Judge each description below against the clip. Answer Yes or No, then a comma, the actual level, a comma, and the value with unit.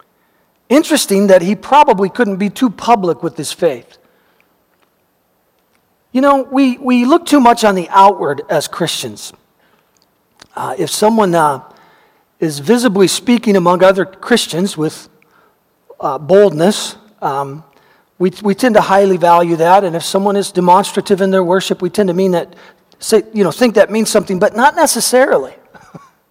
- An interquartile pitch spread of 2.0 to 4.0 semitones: No, average, 4.6 semitones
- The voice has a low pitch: No, high, 200 Hz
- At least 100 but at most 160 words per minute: Yes, average, 155 wpm